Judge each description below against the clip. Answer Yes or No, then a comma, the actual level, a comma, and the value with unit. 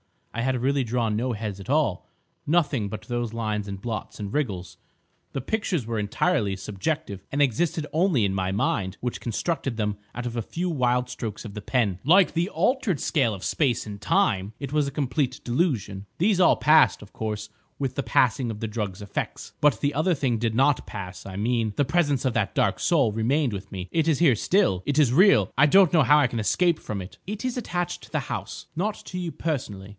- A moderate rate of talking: No, fast, 215 wpm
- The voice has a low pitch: Yes, low, 125 Hz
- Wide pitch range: Yes, wide, 6.4 semitones